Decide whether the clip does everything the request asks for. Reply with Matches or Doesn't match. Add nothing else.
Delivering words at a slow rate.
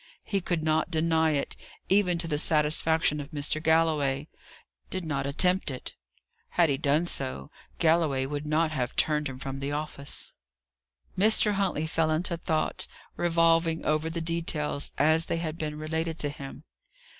Doesn't match